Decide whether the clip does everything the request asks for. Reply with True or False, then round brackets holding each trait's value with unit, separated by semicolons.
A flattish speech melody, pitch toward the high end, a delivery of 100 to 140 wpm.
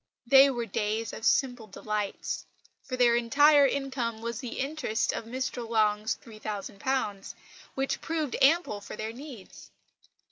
False (3.8 semitones; 235 Hz; 135 wpm)